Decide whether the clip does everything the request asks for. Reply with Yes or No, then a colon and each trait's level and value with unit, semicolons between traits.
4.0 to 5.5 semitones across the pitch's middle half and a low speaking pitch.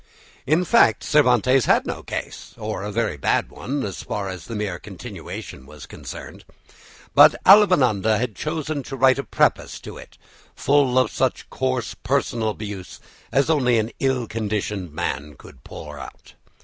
Yes: average, 5.2 semitones; low, 120 Hz